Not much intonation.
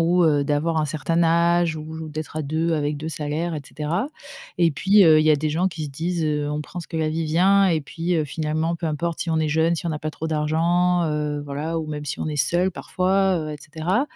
Yes: narrow, 2.0 semitones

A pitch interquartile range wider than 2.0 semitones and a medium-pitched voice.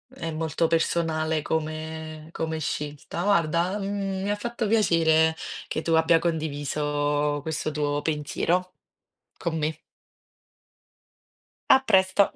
Yes: average, 2.8 semitones; medium, 160 Hz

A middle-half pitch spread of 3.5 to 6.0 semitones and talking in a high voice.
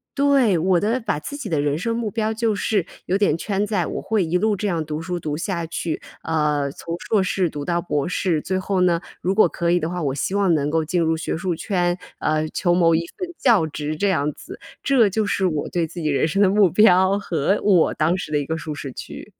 No: average, 4.1 semitones; medium, 175 Hz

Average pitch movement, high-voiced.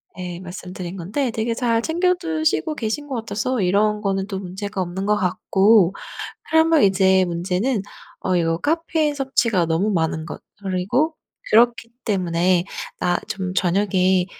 Yes: average, 4.9 semitones; high, 195 Hz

